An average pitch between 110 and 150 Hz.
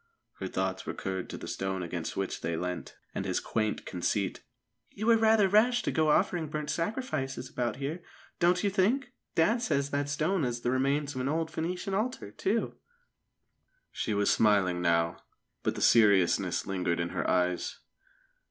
Yes: low, 135 Hz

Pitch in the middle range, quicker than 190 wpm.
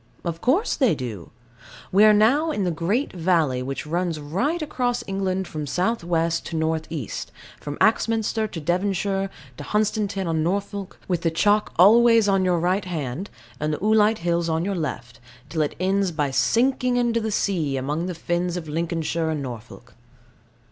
No: medium, 180 Hz; average, 175 wpm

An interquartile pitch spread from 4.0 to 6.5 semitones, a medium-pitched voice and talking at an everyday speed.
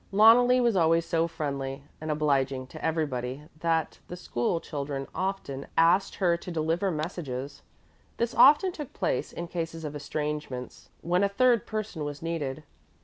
Yes: average, 4.4 semitones; medium, 165 Hz; average, 150 wpm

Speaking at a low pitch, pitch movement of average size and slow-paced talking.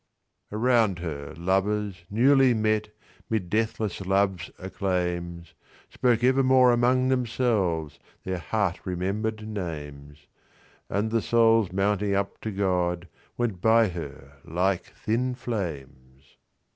Yes: low, 100 Hz; average, 4.4 semitones; slow, 90 wpm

